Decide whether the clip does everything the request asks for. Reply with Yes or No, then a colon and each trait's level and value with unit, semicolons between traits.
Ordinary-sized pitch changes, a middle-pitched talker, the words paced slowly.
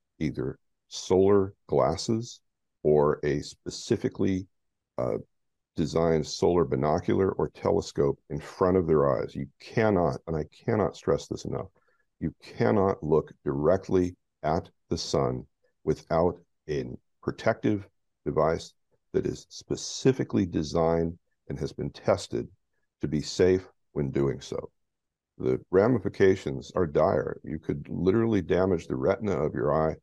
No: average, 4.2 semitones; very low, 85 Hz; slow, 125 wpm